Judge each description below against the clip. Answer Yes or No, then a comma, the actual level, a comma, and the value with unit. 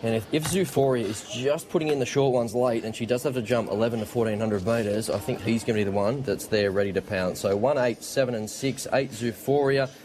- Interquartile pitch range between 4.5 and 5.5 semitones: No, average, 3.9 semitones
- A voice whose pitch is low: Yes, low, 120 Hz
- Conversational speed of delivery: No, fast, 255 wpm